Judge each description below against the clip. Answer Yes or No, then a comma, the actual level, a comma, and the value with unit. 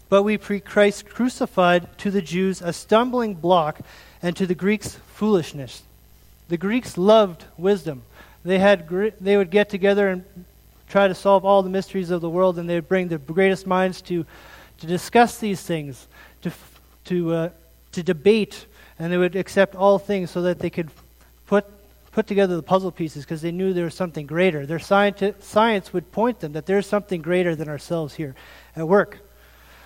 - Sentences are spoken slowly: No, average, 185 wpm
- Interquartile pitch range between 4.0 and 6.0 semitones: No, average, 3.0 semitones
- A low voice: No, medium, 185 Hz